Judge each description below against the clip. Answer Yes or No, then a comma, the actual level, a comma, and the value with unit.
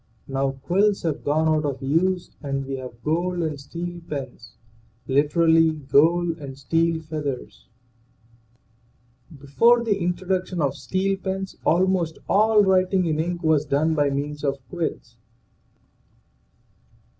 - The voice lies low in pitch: No, medium, 160 Hz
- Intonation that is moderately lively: Yes, average, 4.2 semitones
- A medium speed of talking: No, slow, 125 wpm